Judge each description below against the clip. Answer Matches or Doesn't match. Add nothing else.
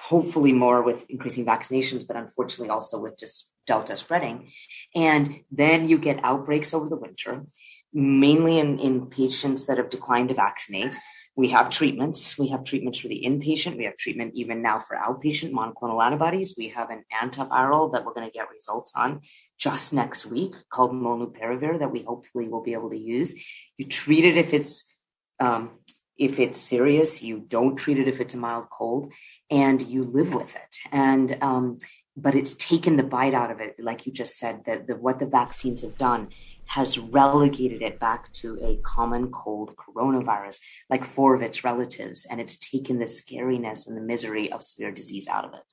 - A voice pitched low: Matches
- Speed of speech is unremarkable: Matches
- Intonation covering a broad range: Doesn't match